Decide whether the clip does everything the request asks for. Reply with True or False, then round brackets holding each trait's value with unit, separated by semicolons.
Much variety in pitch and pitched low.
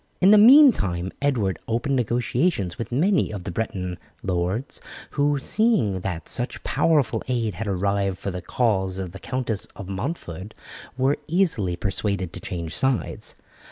True (6.7 semitones; 110 Hz)